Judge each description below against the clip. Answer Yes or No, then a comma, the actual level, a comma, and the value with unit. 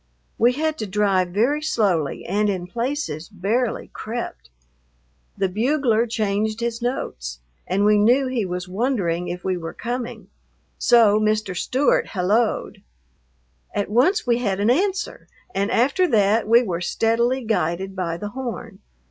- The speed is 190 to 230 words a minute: No, average, 145 wpm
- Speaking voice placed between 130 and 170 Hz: No, high, 215 Hz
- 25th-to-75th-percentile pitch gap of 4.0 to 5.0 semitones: Yes, average, 4.3 semitones